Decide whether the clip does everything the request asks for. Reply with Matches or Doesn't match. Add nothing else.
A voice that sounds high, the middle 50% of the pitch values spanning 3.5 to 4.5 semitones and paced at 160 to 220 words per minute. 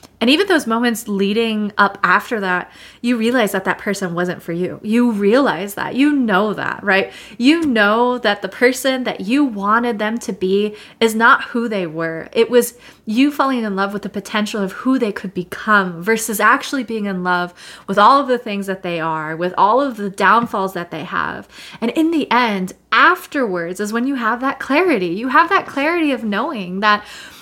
Matches